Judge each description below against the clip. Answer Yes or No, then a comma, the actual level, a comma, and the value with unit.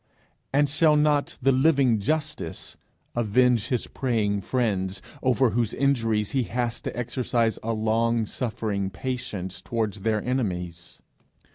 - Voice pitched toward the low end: Yes, low, 115 Hz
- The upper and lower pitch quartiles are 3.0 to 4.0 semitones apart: Yes, average, 3.6 semitones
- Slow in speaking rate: Yes, slow, 125 wpm